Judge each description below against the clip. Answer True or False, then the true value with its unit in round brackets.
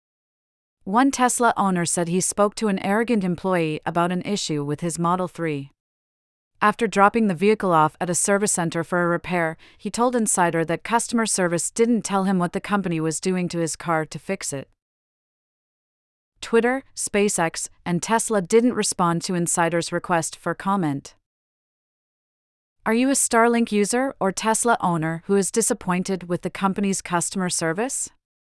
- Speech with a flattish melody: False (4.0 semitones)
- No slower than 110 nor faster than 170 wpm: True (160 wpm)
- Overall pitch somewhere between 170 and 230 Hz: True (185 Hz)